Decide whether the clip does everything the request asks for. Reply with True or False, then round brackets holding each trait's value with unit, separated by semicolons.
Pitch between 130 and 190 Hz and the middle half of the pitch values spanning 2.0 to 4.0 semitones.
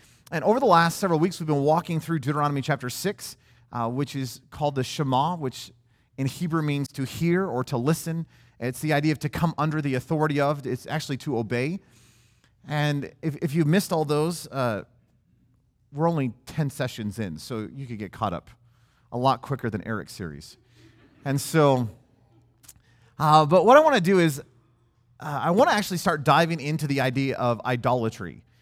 False (135 Hz; 4.5 semitones)